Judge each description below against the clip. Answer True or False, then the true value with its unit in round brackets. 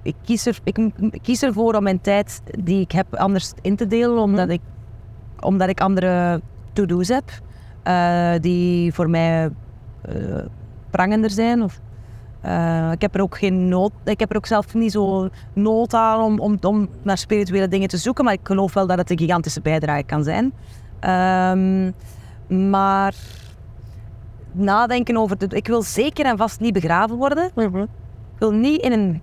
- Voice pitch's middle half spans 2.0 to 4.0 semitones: False (4.9 semitones)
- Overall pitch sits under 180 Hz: False (190 Hz)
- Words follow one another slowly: False (170 wpm)